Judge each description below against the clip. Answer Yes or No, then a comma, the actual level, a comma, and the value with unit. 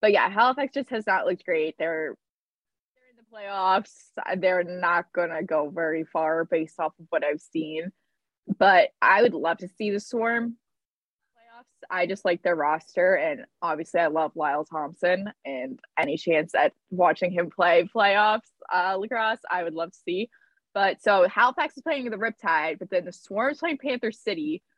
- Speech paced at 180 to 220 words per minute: Yes, average, 185 wpm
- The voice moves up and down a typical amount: No, wide, 5.8 semitones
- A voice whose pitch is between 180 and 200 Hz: Yes, high, 190 Hz